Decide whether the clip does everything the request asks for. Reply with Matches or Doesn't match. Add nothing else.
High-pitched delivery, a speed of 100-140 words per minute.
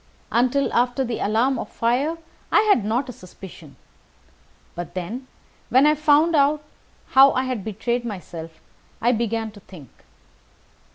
Matches